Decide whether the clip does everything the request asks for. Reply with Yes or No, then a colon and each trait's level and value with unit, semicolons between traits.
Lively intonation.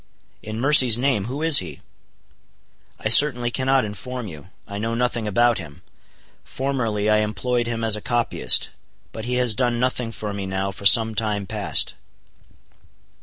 No: average, 3.0 semitones